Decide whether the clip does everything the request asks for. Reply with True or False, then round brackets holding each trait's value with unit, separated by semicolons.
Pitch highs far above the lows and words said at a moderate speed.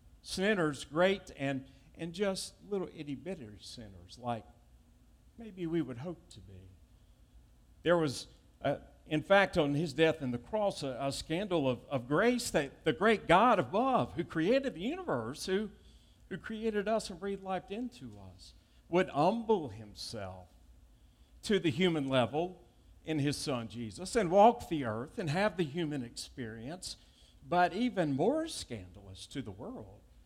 True (8.1 semitones; 155 wpm)